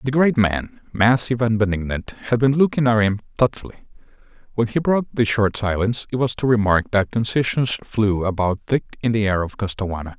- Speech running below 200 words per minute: Yes, average, 190 wpm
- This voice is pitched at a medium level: No, low, 110 Hz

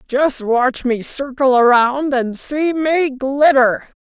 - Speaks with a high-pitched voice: Yes, very high, 265 Hz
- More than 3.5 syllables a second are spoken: No, 3.2 syllables/s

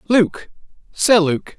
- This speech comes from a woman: No, male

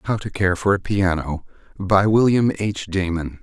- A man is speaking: Yes, male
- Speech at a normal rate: Yes, average, 175 wpm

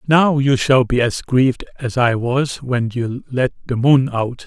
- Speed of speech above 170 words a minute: Yes, average, 200 wpm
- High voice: No, low, 130 Hz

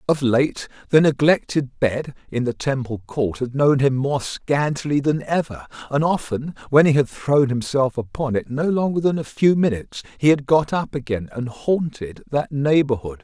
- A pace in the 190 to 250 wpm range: No, average, 180 wpm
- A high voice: No, low, 135 Hz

